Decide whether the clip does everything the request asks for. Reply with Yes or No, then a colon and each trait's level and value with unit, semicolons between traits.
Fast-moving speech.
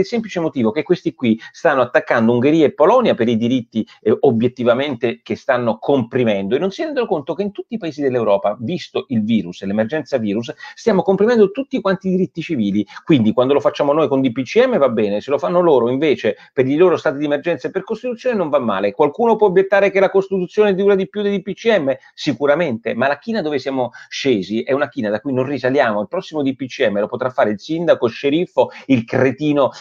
Yes: fast, 210 wpm